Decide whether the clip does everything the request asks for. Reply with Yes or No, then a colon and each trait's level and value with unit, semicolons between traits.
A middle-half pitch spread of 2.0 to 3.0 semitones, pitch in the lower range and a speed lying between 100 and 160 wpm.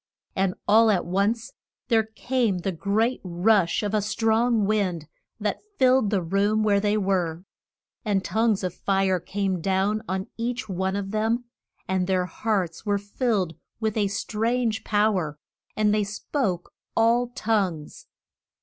No: average, 2.7 semitones; high, 205 Hz; average, 150 wpm